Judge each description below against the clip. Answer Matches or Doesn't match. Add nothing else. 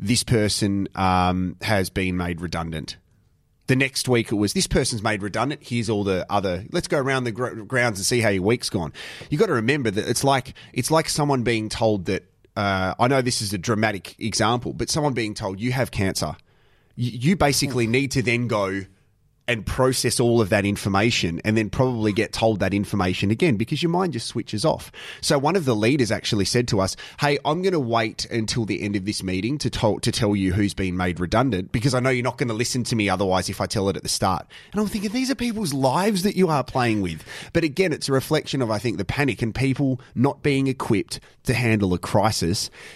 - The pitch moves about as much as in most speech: Matches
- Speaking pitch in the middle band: Doesn't match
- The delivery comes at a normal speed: Doesn't match